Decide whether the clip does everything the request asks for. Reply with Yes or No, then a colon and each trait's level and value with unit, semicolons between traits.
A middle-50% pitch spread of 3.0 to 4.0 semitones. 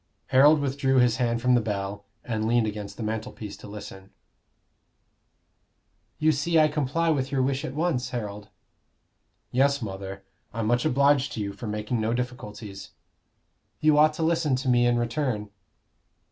No: average, 4.8 semitones